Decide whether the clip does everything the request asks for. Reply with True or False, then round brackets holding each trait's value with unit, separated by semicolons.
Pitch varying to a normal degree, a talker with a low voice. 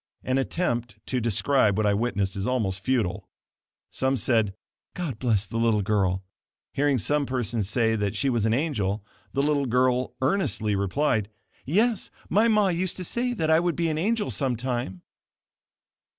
False (5.9 semitones; 125 Hz)